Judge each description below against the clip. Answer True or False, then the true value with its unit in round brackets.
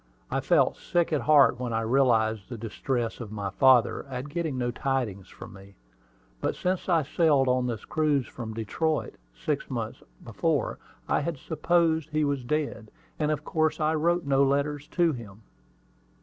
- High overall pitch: False (135 Hz)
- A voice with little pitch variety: False (4.7 semitones)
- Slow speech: False (170 wpm)